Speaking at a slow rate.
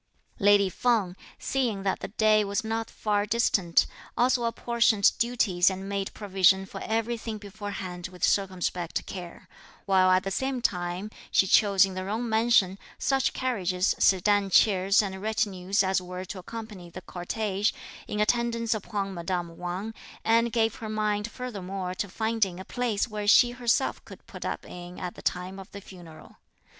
No: average, 160 wpm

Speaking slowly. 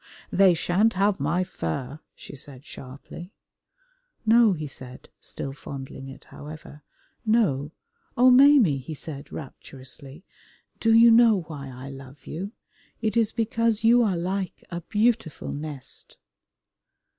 Yes: slow, 130 wpm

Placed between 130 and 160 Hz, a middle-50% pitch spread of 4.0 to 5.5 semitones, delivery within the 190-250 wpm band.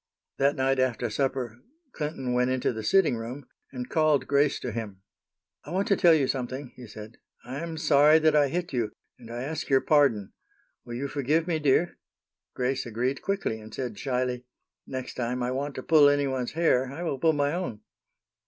No: low, 135 Hz; average, 3.3 semitones; average, 195 wpm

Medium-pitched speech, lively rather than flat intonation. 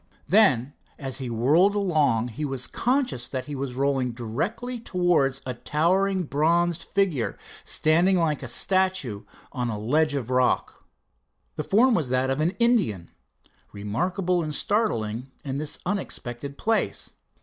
Yes: medium, 150 Hz; wide, 6.7 semitones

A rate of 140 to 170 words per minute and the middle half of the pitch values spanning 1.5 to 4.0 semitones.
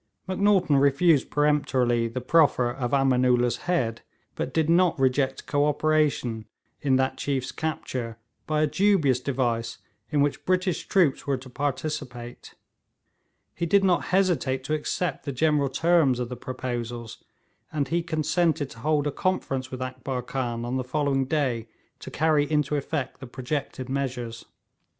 Yes: average, 150 wpm; average, 3.5 semitones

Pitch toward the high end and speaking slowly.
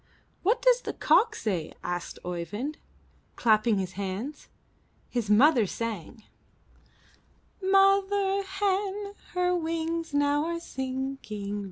Yes: very high, 290 Hz; slow, 100 wpm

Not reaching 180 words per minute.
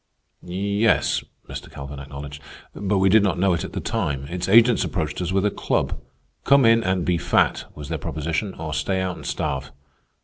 No: average, 195 wpm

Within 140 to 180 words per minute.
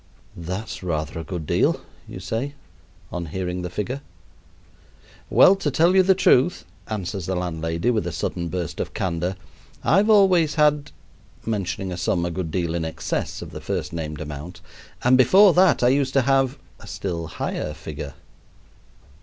Yes: average, 165 wpm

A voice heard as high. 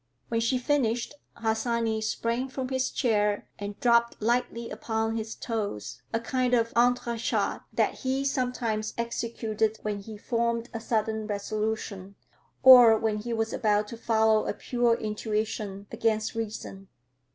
Yes: high, 225 Hz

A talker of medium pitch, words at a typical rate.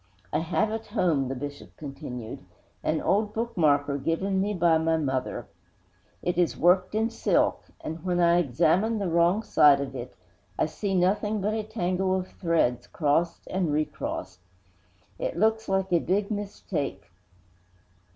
Yes: medium, 175 Hz; average, 150 wpm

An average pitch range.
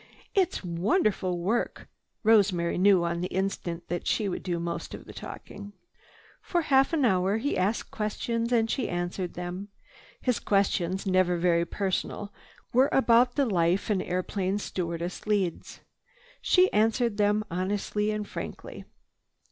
Yes: average, 3.9 semitones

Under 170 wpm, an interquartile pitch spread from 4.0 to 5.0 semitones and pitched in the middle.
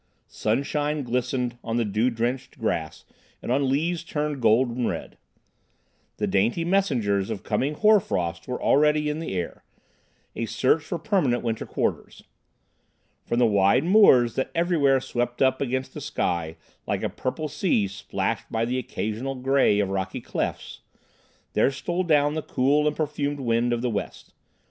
No: average, 160 wpm; average, 4.5 semitones; low, 130 Hz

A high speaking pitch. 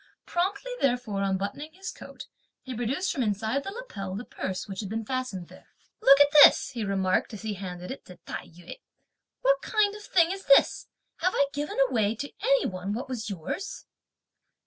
Yes: high, 245 Hz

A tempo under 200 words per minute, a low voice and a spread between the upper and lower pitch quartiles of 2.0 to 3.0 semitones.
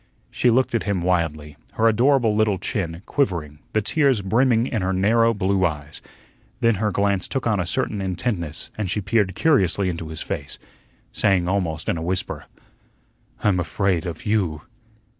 No: average, 165 wpm; very low, 95 Hz; average, 4.4 semitones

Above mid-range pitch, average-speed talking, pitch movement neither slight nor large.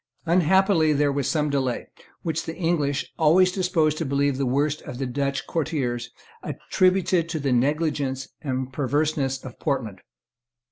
No: medium, 145 Hz; average, 145 wpm; average, 3.4 semitones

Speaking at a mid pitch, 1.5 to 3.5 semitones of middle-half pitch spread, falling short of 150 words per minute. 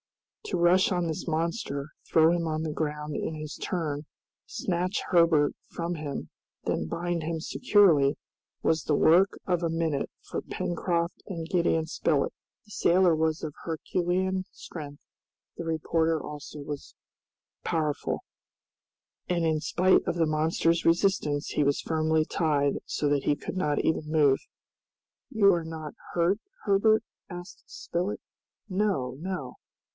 Yes: medium, 165 Hz; narrow, 2.6 semitones; average, 140 wpm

